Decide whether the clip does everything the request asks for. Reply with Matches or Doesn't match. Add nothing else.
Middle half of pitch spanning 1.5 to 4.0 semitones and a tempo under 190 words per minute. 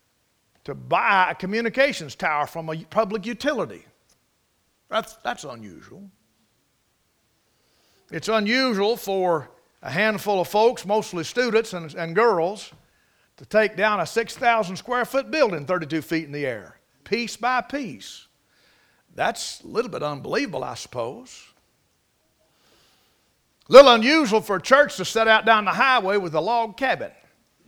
Doesn't match